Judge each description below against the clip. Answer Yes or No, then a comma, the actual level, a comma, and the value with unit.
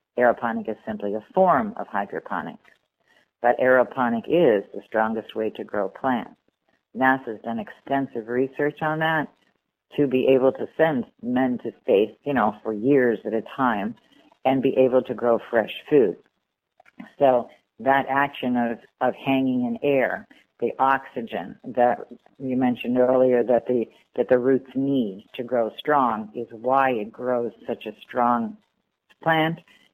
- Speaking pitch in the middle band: No, low, 125 Hz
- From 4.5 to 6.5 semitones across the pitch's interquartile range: No, narrow, 2.4 semitones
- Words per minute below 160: Yes, average, 150 wpm